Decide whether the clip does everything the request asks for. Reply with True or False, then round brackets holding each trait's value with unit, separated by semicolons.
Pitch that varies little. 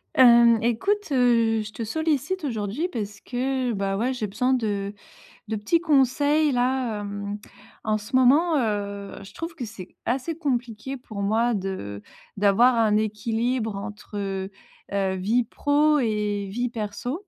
False (4.2 semitones)